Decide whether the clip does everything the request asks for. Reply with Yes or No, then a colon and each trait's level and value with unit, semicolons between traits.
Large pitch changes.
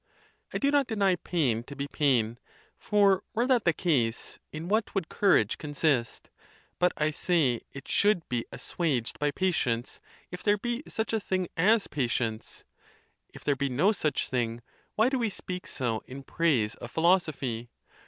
Yes: wide, 7.9 semitones